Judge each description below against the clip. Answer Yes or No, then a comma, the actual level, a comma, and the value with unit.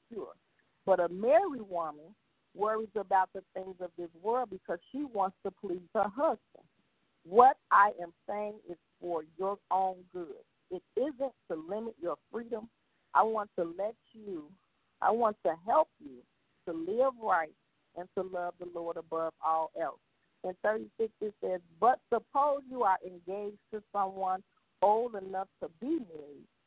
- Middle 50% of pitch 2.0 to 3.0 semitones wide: No, average, 4.0 semitones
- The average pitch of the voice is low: No, high, 195 Hz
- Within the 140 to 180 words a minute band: Yes, average, 155 wpm